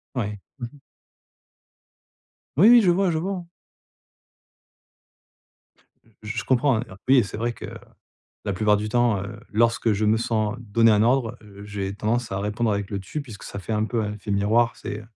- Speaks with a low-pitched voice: Yes, low, 110 Hz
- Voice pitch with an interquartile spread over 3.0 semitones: No, narrow, 2.6 semitones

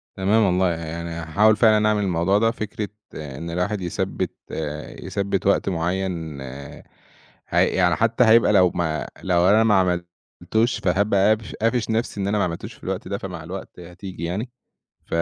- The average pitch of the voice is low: Yes, very low, 95 Hz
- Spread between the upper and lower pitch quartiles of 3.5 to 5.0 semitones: Yes, average, 3.9 semitones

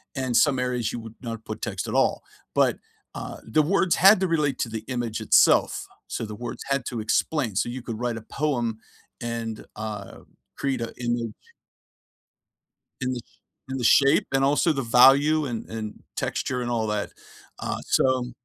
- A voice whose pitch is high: No, low, 120 Hz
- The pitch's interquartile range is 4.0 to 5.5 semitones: No, average, 3.3 semitones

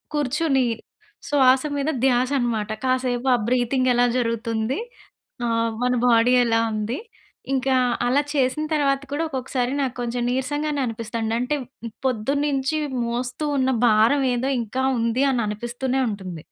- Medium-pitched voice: No, very high, 250 Hz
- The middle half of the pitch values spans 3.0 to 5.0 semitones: No, narrow, 2.6 semitones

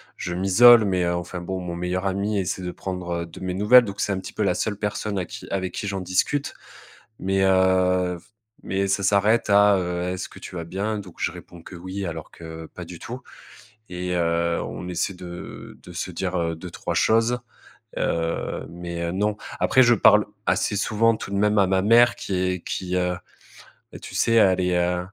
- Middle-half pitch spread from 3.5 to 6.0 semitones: No, narrow, 2.4 semitones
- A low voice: Yes, very low, 95 Hz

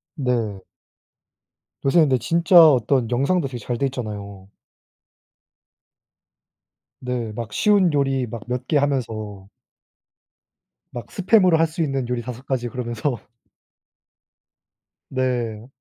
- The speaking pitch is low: Yes, low, 125 Hz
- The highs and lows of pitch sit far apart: No, average, 3.5 semitones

